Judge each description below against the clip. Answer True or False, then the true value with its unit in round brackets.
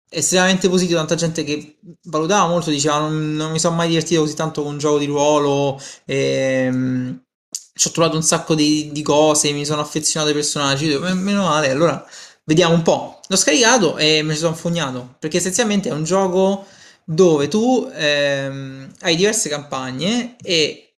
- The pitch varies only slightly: False (3.8 semitones)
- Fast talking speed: True (175 wpm)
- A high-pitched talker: False (155 Hz)